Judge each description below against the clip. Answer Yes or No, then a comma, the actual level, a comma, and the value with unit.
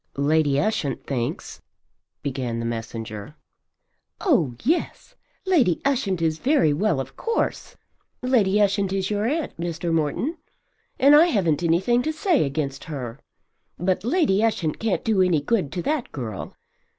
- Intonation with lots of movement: Yes, wide, 8.9 semitones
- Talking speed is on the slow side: No, average, 145 wpm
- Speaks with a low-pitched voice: No, medium, 180 Hz